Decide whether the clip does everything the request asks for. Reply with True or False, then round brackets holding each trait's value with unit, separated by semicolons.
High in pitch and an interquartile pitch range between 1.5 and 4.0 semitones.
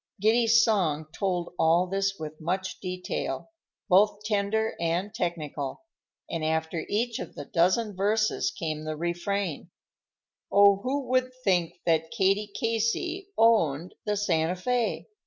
False (195 Hz; 4.7 semitones)